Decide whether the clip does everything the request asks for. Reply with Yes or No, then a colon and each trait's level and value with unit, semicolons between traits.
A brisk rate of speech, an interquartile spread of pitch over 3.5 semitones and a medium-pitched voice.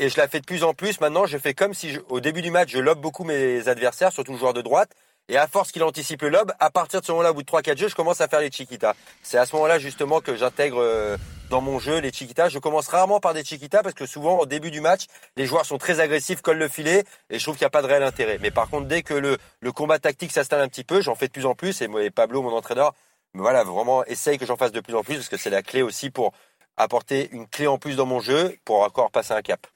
Yes: fast, 300 wpm; average, 4.3 semitones; medium, 145 Hz